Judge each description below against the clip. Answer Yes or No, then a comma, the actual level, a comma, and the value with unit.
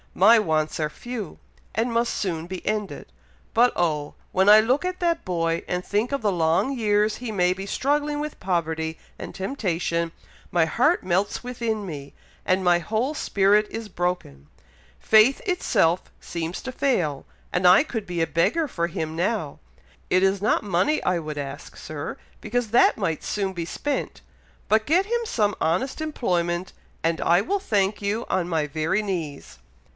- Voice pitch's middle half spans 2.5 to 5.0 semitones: No, wide, 5.6 semitones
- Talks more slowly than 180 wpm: Yes, average, 170 wpm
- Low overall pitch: No, high, 190 Hz